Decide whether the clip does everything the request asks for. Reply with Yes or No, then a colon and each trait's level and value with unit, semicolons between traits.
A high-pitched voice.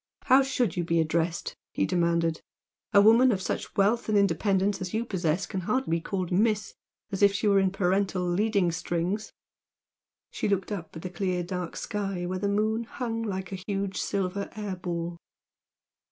Yes: high, 195 Hz